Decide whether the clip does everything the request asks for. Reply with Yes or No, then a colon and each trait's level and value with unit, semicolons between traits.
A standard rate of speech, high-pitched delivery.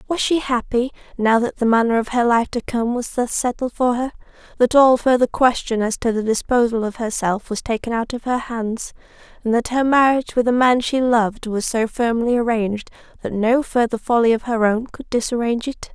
No: fast, 210 wpm; high, 235 Hz